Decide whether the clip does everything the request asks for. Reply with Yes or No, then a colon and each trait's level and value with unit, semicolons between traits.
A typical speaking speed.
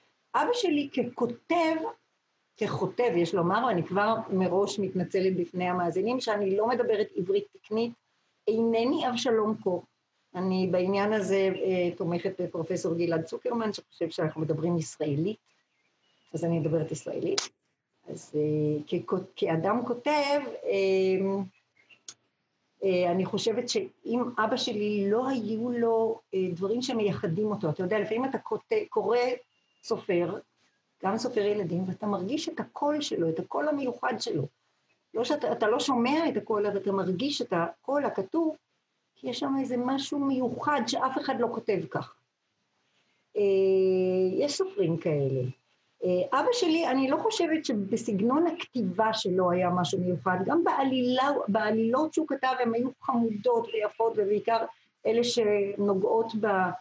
Yes: average, 135 wpm